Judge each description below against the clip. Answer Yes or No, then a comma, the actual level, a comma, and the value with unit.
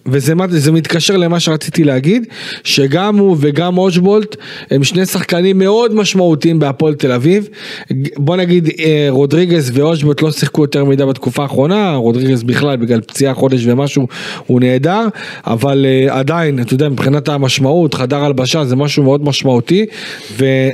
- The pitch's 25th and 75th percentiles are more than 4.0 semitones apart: Yes, average, 4.5 semitones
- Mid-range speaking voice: Yes, medium, 150 Hz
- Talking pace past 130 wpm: Yes, average, 140 wpm